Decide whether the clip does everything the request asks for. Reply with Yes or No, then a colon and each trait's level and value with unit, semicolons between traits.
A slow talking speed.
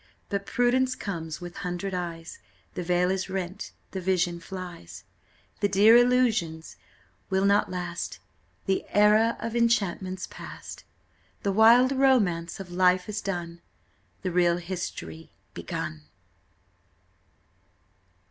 Yes: slow, 115 wpm